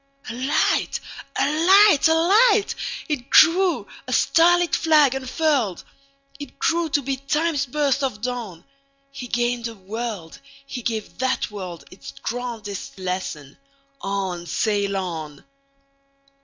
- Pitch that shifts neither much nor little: No, wide, 6.6 semitones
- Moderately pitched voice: No, very high, 260 Hz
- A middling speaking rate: No, slow, 110 wpm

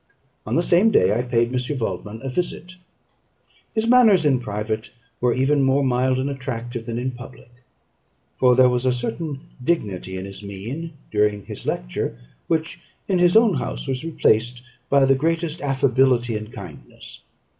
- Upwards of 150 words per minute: Yes, average, 165 wpm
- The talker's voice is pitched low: Yes, low, 125 Hz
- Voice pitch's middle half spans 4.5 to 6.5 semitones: Yes, average, 4.8 semitones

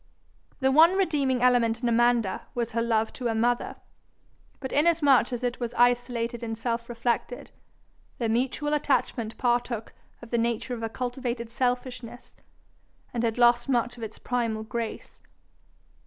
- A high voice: Yes, high, 240 Hz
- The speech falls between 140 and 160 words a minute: Yes, average, 150 wpm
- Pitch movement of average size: No, narrow, 1.4 semitones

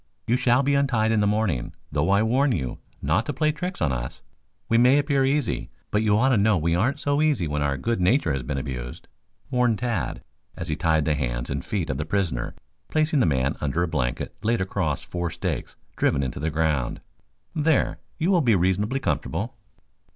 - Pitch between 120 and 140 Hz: No, low, 100 Hz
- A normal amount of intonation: No, wide, 9.0 semitones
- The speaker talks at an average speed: No, fast, 210 wpm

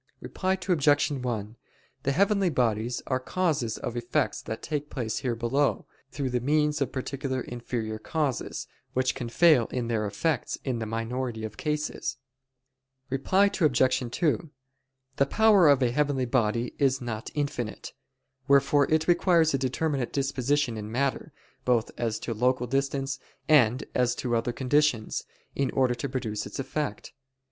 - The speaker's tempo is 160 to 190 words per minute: No, average, 150 wpm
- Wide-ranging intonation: No, average, 3.7 semitones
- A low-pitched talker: Yes, low, 130 Hz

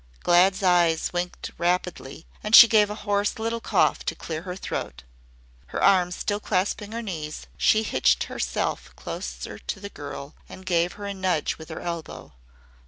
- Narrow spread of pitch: No, average, 3.5 semitones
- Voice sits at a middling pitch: Yes, medium, 180 Hz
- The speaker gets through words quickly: No, average, 170 wpm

